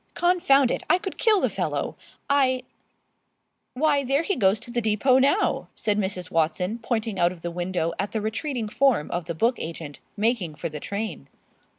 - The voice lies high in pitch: Yes, high, 220 Hz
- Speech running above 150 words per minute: Yes, average, 190 wpm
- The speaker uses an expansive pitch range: Yes, wide, 7.3 semitones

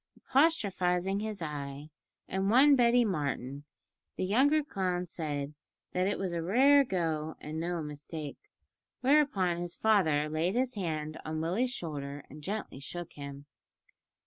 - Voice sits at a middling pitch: Yes, medium, 175 Hz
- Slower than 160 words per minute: Yes, average, 140 wpm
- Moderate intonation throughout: No, wide, 6.1 semitones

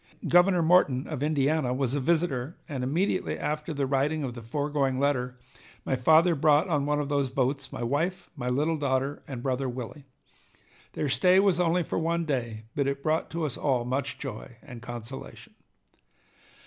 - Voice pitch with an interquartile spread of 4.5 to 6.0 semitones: No, average, 3.5 semitones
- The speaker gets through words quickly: No, average, 175 wpm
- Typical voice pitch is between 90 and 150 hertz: Yes, medium, 140 Hz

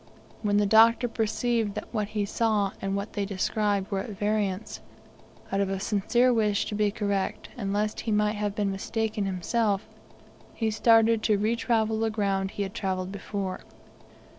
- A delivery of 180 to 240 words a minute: No, average, 170 wpm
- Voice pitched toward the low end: No, high, 210 Hz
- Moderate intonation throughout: No, narrow, 2.0 semitones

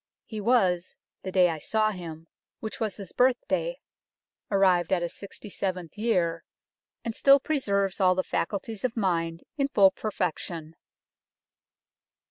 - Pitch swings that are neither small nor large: Yes, average, 3.9 semitones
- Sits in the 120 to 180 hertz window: No, high, 195 Hz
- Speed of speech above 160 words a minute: No, average, 150 wpm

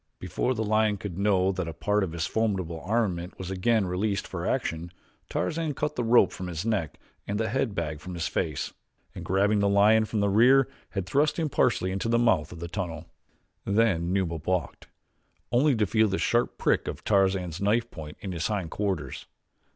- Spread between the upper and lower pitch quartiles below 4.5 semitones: Yes, average, 3.8 semitones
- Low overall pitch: Yes, low, 100 Hz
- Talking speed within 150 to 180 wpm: No, average, 200 wpm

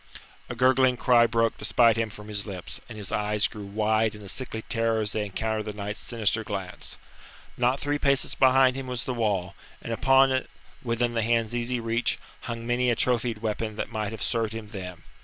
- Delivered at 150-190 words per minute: No, fast, 205 wpm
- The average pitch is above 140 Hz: No, low, 115 Hz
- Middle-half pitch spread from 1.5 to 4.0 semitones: Yes, narrow, 2.5 semitones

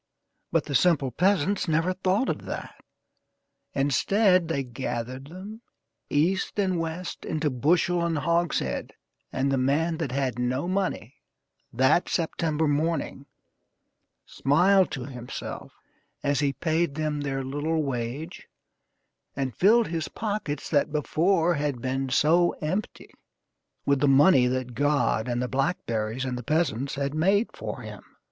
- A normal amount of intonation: Yes, average, 4.4 semitones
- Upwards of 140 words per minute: No, slow, 135 wpm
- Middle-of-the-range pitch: Yes, medium, 150 Hz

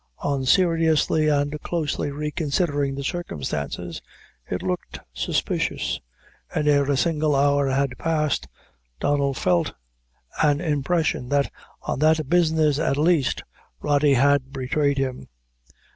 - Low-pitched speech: No, medium, 145 Hz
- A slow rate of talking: Yes, slow, 115 wpm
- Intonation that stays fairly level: Yes, narrow, 2.2 semitones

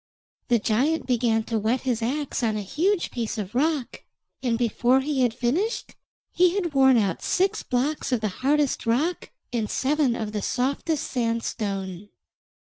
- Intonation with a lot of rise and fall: No, average, 4.6 semitones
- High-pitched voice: Yes, high, 245 Hz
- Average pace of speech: Yes, average, 160 wpm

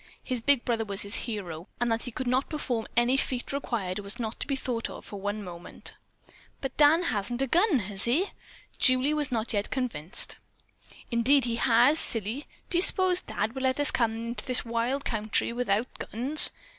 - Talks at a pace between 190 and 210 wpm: Yes, average, 195 wpm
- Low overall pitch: No, high, 240 Hz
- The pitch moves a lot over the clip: No, average, 3.8 semitones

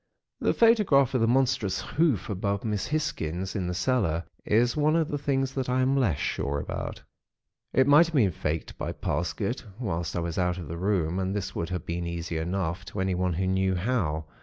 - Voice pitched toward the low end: Yes, very low, 95 Hz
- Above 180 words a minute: Yes, fast, 205 wpm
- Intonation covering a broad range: Yes, wide, 6.9 semitones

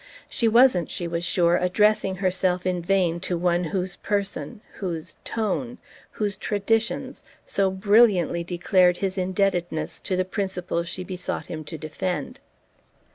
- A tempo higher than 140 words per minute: No, slow, 135 wpm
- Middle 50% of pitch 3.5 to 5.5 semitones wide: No, narrow, 2.4 semitones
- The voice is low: No, medium, 185 Hz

